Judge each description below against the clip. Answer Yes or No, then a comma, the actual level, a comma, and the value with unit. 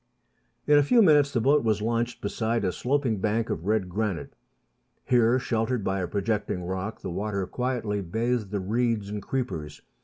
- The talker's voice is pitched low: Yes, low, 110 Hz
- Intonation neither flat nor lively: Yes, average, 3.7 semitones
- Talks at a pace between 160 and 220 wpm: Yes, average, 175 wpm